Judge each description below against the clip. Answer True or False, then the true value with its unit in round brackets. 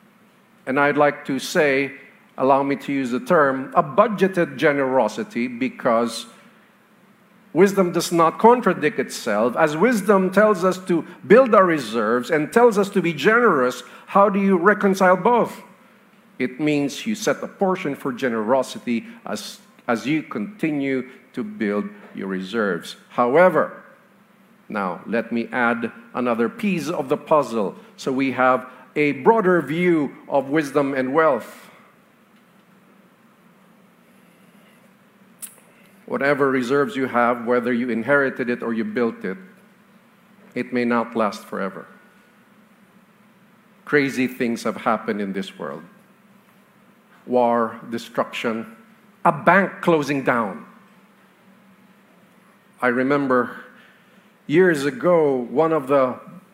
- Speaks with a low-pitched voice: False (185 Hz)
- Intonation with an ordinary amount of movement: False (7.8 semitones)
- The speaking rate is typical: False (120 wpm)